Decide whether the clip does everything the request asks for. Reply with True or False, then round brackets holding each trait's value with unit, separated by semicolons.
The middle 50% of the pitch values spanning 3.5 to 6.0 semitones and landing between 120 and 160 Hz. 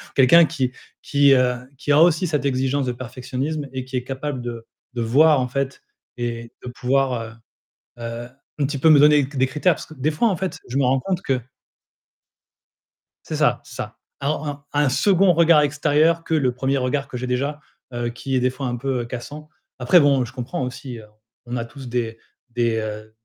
False (3.1 semitones; 135 Hz)